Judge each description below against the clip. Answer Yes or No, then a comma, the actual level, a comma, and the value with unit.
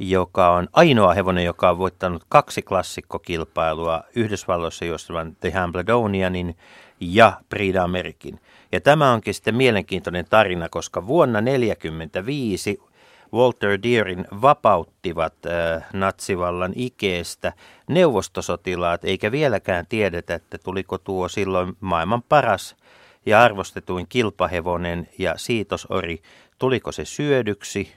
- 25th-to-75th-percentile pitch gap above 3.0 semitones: No, narrow, 2.5 semitones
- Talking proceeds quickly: No, average, 105 wpm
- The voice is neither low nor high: No, very low, 90 Hz